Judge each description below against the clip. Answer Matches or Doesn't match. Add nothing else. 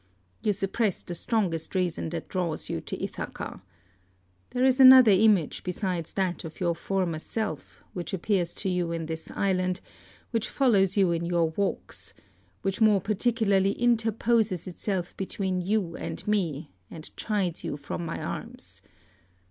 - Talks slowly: Doesn't match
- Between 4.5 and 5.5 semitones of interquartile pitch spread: Doesn't match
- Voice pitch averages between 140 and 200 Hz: Matches